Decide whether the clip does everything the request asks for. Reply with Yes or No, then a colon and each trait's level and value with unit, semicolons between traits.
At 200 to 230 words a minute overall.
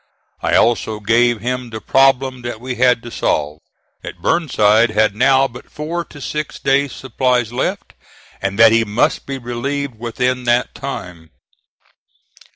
No: average, 150 wpm